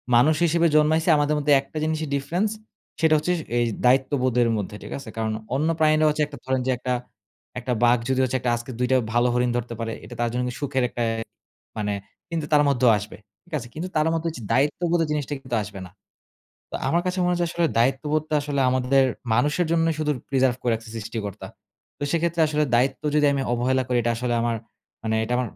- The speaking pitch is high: No, low, 135 Hz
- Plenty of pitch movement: No, average, 4.1 semitones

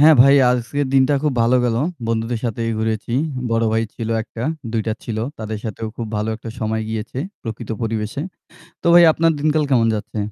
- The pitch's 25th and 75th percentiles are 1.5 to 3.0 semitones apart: Yes, average, 2.7 semitones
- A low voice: Yes, low, 115 Hz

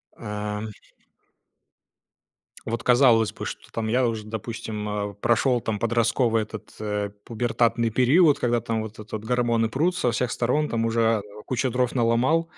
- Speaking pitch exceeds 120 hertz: No, low, 115 Hz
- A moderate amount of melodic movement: No, narrow, 2.0 semitones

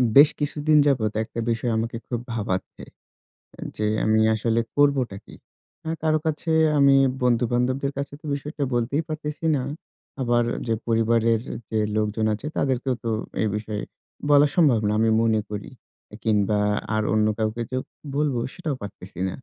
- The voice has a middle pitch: No, low, 120 Hz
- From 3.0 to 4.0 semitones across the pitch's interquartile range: No, average, 4.5 semitones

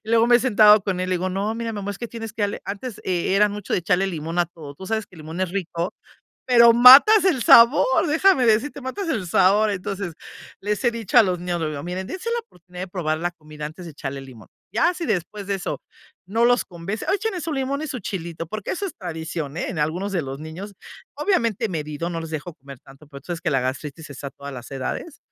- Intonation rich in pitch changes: Yes, wide, 6.0 semitones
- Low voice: No, high, 190 Hz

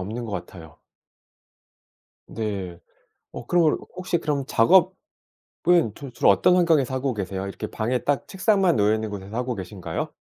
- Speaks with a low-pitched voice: Yes, low, 120 Hz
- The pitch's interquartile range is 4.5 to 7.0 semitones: No, wide, 7.8 semitones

